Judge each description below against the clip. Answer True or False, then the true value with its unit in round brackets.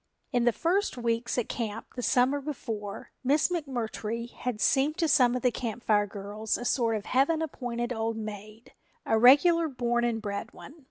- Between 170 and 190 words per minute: True (180 wpm)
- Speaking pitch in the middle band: False (240 Hz)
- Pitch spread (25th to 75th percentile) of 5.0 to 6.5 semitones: False (3.3 semitones)